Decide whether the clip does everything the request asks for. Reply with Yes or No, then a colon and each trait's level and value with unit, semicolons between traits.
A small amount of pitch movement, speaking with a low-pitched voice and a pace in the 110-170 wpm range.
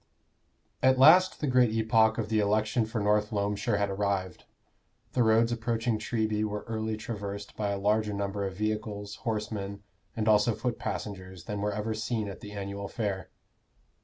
Yes: narrow, 1.7 semitones; low, 105 Hz; average, 165 wpm